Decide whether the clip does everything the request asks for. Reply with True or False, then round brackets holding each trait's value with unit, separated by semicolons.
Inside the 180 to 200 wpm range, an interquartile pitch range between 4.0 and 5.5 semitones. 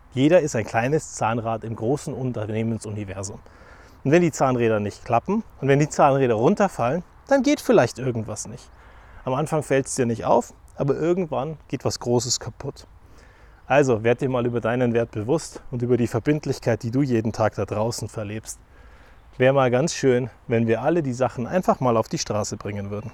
True (185 wpm; 4.4 semitones)